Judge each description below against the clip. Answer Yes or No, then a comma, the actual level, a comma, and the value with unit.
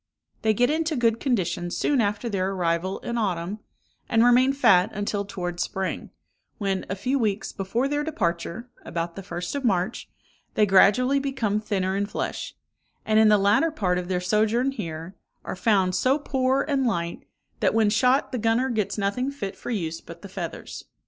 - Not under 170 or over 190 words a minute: Yes, average, 180 wpm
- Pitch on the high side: Yes, high, 210 Hz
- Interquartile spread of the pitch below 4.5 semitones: No, average, 5.0 semitones